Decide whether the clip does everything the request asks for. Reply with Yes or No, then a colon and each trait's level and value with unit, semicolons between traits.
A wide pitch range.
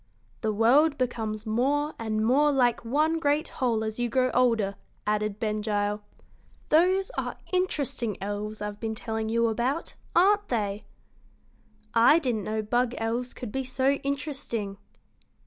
No: average, 4.5 semitones